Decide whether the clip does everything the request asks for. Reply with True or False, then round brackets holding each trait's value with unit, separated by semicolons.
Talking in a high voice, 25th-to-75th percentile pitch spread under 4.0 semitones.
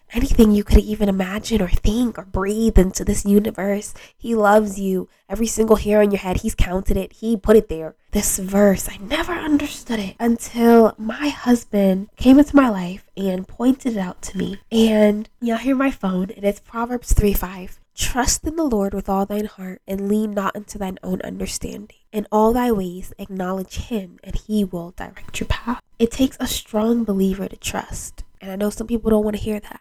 True (210 Hz; 2.9 semitones)